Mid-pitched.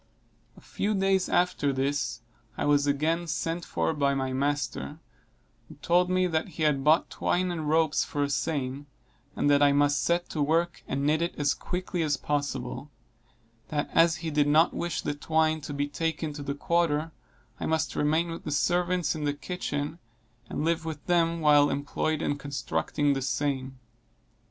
Yes: medium, 150 Hz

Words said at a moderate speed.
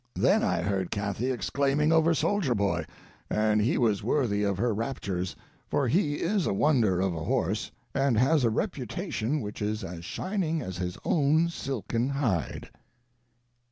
Yes: average, 160 wpm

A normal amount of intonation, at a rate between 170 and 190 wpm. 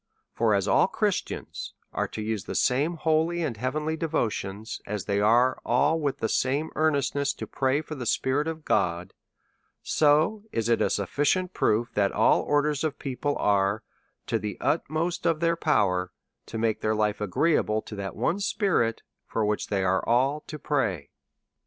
No: wide, 6.5 semitones; average, 175 wpm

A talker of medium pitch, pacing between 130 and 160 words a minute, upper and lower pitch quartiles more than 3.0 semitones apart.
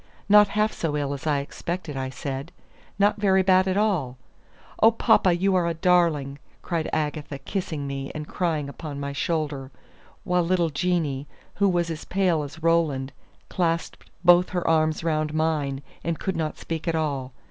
No: medium, 160 Hz; average, 170 wpm; average, 3.7 semitones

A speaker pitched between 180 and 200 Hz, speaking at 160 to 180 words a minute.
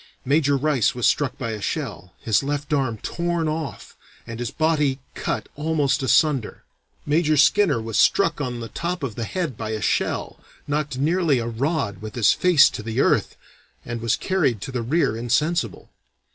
No: medium, 140 Hz; average, 175 wpm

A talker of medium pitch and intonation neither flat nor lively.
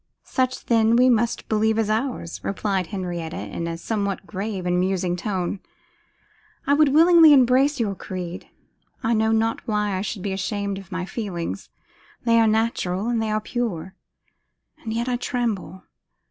No: high, 215 Hz; average, 3.9 semitones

